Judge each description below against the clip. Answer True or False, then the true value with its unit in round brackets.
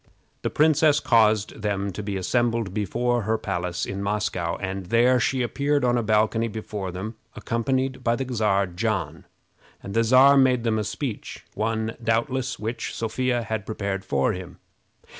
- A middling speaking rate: True (160 wpm)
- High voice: False (110 Hz)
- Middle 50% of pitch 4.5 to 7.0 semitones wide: False (3.6 semitones)